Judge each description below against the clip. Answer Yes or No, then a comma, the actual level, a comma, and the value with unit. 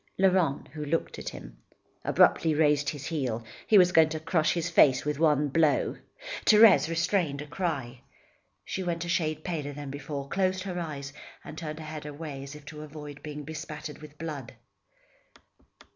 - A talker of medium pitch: Yes, medium, 155 Hz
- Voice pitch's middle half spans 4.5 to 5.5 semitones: No, narrow, 2.4 semitones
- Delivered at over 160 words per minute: Yes, average, 175 wpm